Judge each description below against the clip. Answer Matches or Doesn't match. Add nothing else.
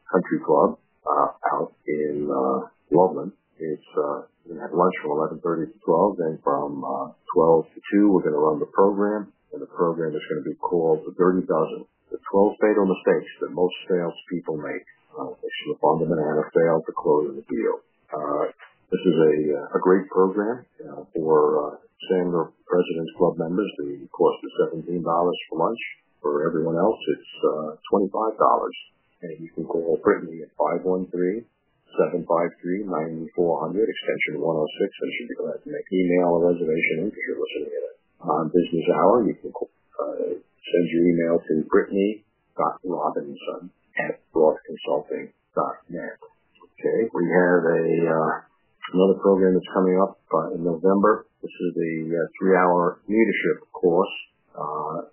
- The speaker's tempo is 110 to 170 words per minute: Matches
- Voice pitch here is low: Matches